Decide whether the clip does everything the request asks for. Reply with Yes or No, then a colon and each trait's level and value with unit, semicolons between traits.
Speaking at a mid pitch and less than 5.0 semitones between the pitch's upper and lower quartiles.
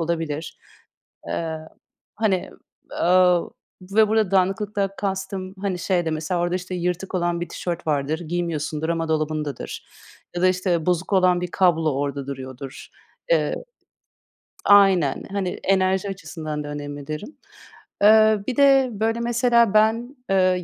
Yes: medium, 180 Hz; average, 3.8 semitones